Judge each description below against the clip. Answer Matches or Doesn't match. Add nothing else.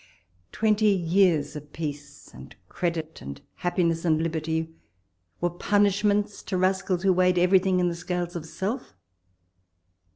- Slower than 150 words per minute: Matches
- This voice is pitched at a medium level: Matches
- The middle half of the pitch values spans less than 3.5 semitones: Matches